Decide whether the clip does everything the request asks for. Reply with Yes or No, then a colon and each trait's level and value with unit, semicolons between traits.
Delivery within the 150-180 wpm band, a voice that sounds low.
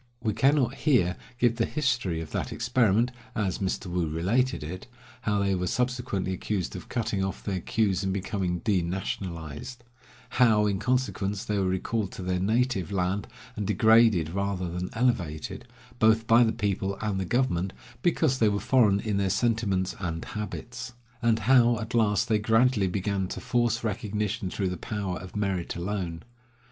Yes: average, 170 wpm; low, 105 Hz